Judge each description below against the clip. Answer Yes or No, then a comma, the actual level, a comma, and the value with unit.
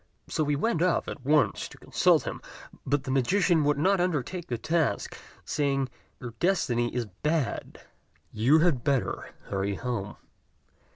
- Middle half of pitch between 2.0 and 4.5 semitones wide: No, average, 5.2 semitones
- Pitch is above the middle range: No, medium, 145 Hz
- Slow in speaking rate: No, average, 150 wpm